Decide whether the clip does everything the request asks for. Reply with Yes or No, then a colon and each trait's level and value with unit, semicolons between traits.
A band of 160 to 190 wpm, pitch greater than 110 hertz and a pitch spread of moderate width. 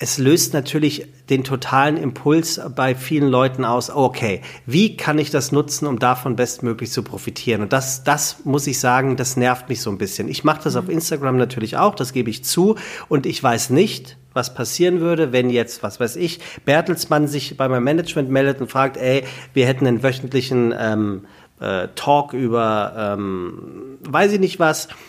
Yes: average, 185 wpm; low, 135 Hz; average, 3.4 semitones